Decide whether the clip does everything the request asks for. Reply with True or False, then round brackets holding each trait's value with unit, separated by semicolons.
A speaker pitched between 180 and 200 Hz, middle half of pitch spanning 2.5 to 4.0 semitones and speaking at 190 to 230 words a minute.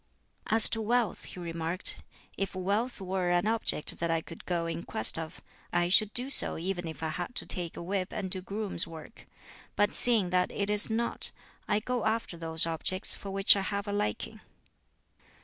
True (190 Hz; 3.7 semitones; 195 wpm)